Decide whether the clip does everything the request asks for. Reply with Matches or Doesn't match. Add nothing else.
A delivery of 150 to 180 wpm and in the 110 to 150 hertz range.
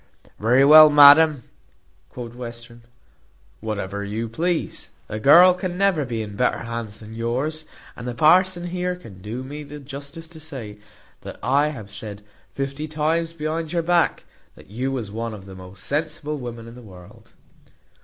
Matches